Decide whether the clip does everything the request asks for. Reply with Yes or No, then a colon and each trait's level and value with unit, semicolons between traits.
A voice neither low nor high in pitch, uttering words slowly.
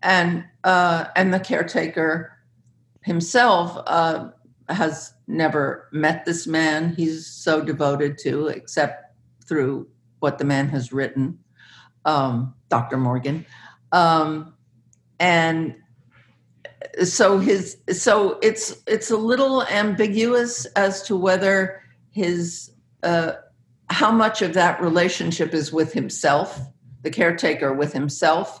Yes: medium, 160 Hz; slow, 110 wpm